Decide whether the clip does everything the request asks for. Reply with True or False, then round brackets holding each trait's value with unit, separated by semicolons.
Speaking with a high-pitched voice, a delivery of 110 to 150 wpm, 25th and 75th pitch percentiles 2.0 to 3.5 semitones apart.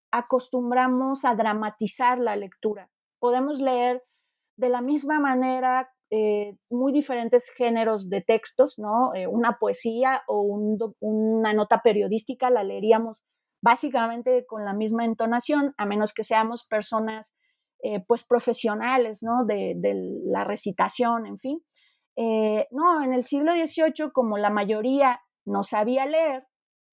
True (240 Hz; 135 wpm; 3.1 semitones)